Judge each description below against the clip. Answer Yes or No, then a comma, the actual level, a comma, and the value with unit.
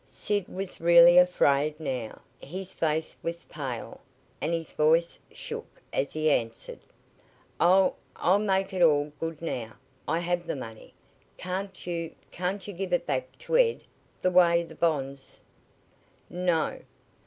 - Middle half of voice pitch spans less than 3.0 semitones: No, average, 3.5 semitones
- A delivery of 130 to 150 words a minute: Yes, average, 145 wpm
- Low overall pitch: No, medium, 170 Hz